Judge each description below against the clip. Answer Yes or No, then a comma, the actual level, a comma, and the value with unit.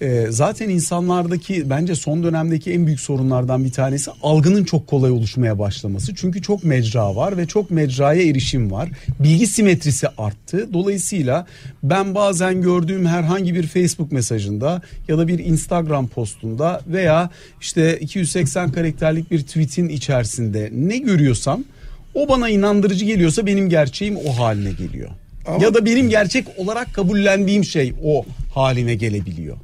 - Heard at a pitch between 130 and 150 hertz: No, medium, 160 Hz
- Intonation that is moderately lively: No, wide, 5.8 semitones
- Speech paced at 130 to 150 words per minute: Yes, fast, 140 wpm